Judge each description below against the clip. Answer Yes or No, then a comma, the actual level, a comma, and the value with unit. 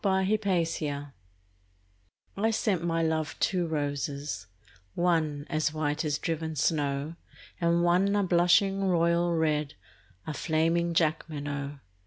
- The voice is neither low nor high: Yes, medium, 165 Hz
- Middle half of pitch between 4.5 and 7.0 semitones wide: No, average, 2.7 semitones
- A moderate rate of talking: No, slow, 120 wpm